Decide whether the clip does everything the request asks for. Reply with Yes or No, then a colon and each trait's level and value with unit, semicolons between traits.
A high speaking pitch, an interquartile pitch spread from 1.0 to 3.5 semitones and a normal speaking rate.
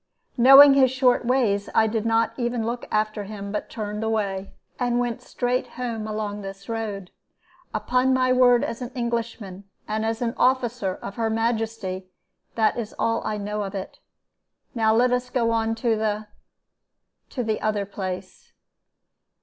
Yes: high, 225 Hz; narrow, 2.6 semitones; average, 160 wpm